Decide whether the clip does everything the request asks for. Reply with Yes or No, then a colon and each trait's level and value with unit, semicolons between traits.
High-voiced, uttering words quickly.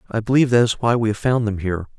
No: low, 115 Hz; fast, 300 wpm